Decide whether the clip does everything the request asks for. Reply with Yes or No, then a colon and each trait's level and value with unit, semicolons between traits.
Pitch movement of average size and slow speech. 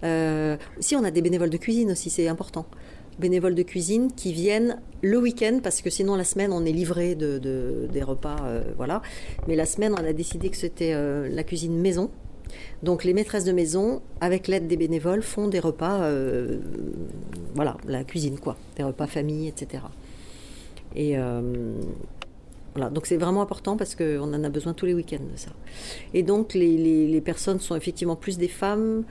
No: average, 4.0 semitones; average, 190 wpm